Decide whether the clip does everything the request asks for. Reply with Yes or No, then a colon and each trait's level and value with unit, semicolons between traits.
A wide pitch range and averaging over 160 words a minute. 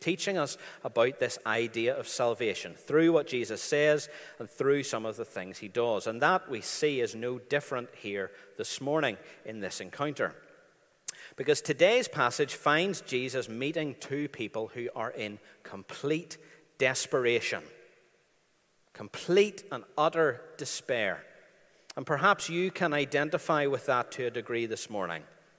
No: wide, 7.2 semitones; average, 145 wpm